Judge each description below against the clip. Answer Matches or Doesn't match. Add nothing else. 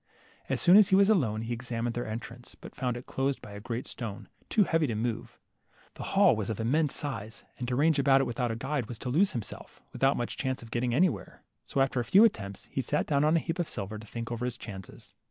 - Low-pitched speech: Matches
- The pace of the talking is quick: Matches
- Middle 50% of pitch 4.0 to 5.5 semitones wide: Matches